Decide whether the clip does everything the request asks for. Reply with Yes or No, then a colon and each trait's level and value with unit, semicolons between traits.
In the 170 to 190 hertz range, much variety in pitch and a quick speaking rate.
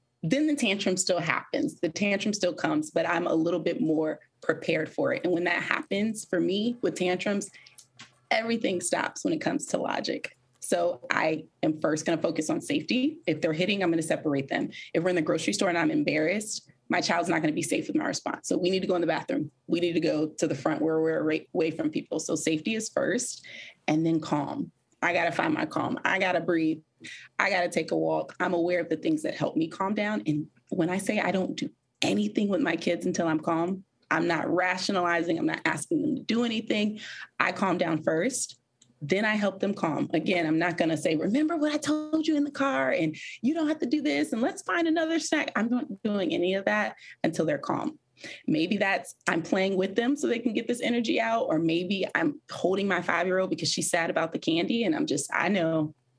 Yes: medium, 185 Hz; wide, 7.4 semitones; fast, 235 wpm